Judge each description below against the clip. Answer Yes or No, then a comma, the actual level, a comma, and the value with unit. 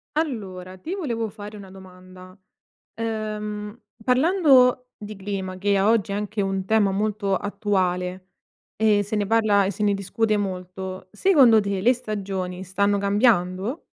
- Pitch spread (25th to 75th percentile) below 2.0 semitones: No, narrow, 2.6 semitones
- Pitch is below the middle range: No, high, 205 Hz